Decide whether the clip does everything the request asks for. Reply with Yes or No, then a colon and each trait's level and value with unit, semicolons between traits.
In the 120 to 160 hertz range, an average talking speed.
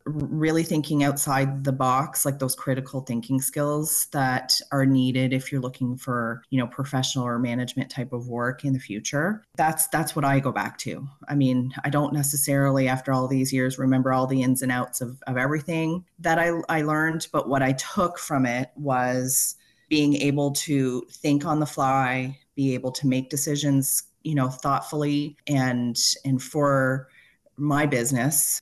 Yes: low, 135 Hz; average, 175 wpm